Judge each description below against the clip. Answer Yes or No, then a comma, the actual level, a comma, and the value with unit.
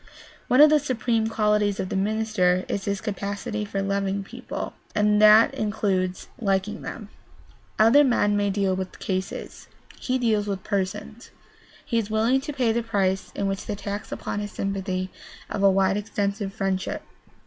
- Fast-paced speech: No, average, 160 wpm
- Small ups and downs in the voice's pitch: Yes, narrow, 2.2 semitones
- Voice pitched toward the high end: Yes, high, 205 Hz